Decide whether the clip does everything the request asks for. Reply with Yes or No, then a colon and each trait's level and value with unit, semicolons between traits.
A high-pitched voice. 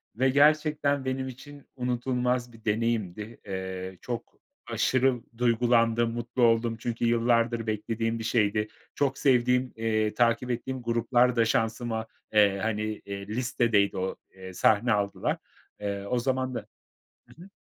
No: low, 115 Hz